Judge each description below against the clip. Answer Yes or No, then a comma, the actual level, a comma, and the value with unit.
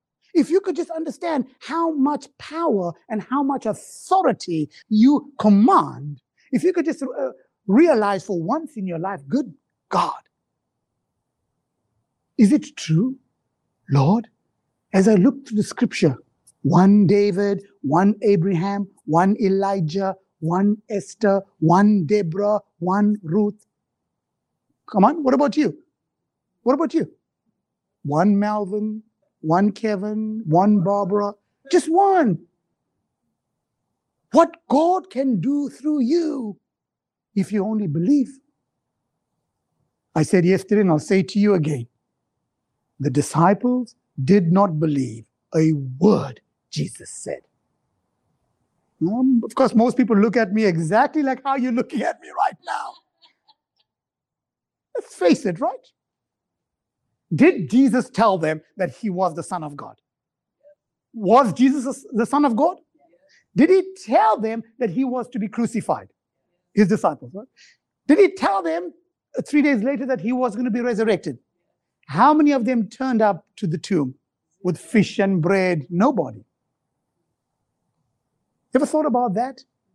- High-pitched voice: Yes, high, 215 Hz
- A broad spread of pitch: Yes, wide, 6.0 semitones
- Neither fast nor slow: No, slow, 130 wpm